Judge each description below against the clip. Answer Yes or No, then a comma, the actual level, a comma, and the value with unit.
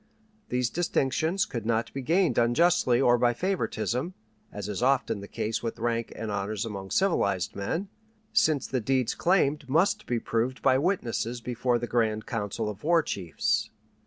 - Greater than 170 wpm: No, average, 160 wpm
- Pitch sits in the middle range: No, low, 120 Hz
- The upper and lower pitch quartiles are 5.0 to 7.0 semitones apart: Yes, wide, 5.6 semitones